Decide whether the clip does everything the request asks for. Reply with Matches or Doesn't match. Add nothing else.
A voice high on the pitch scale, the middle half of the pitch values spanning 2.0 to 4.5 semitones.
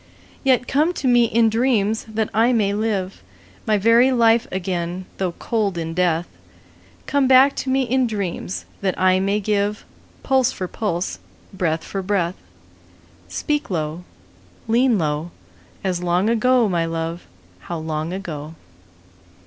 Doesn't match